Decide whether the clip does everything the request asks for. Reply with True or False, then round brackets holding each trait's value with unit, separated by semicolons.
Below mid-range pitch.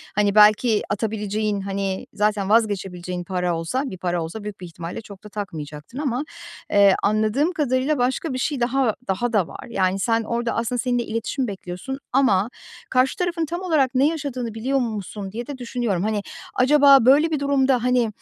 False (225 Hz)